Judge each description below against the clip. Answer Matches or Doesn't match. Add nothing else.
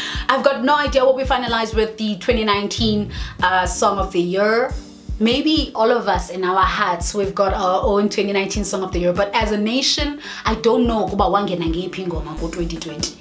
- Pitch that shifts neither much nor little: Matches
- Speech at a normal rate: Matches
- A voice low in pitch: Doesn't match